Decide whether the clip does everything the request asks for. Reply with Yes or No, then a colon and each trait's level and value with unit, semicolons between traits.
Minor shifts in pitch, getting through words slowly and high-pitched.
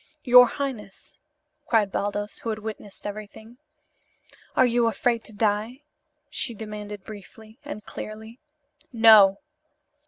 Yes: narrow, 2.1 semitones; slow, 115 wpm; high, 220 Hz